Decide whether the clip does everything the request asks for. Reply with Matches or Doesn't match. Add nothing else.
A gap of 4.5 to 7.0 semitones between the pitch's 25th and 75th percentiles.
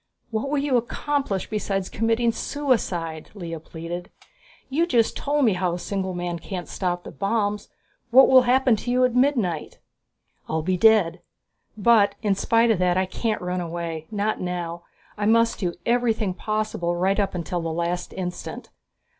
Matches